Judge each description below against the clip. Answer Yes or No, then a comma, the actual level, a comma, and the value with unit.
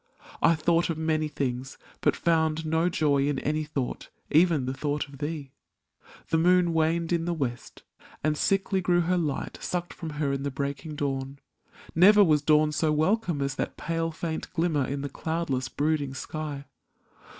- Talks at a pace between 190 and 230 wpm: No, average, 175 wpm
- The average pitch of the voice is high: No, medium, 155 Hz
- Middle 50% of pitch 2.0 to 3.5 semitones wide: Yes, average, 2.9 semitones